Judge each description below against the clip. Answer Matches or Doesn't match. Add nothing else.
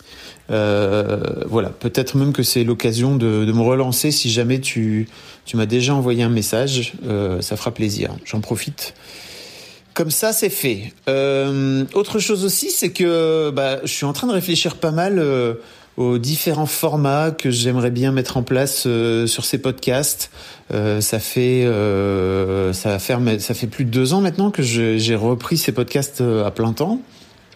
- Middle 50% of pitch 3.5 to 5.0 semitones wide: Matches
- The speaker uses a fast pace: Doesn't match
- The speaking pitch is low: Matches